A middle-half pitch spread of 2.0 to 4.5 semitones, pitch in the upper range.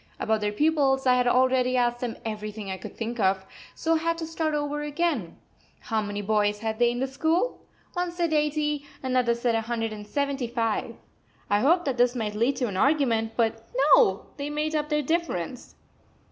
No: average, 5.1 semitones; very high, 250 Hz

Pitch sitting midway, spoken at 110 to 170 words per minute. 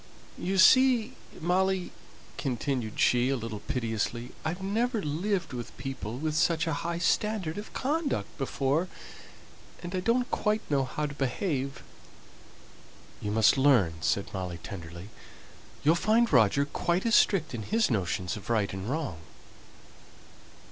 Yes: medium, 145 Hz; average, 140 wpm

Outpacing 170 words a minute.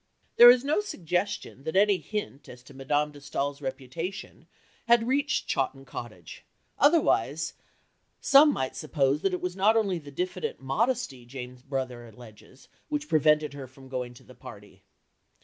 No: average, 155 wpm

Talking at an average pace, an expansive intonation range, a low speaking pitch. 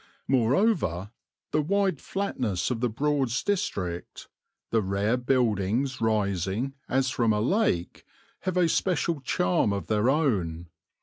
No: slow, 125 wpm; wide, 6.8 semitones; low, 120 Hz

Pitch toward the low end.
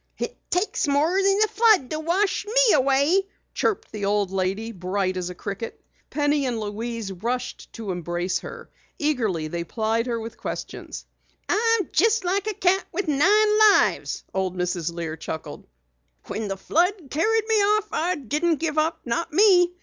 No: very high, 285 Hz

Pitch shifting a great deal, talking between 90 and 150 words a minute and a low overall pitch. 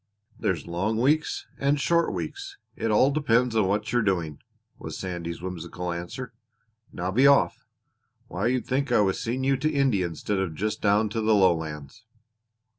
No: wide, 6.6 semitones; average, 170 wpm; low, 105 Hz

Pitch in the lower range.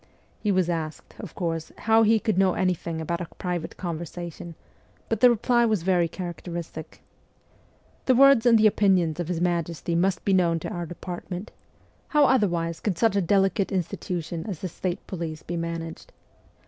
No: medium, 180 Hz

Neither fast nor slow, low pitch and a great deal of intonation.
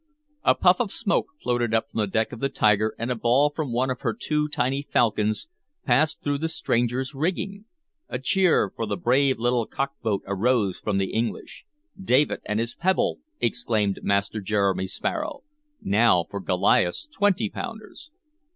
Yes: average, 165 wpm; low, 125 Hz; wide, 5.8 semitones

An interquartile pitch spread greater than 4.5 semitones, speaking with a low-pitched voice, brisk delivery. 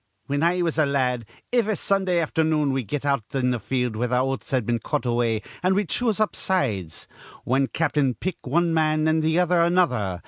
No: wide, 5.4 semitones; medium, 145 Hz; fast, 210 wpm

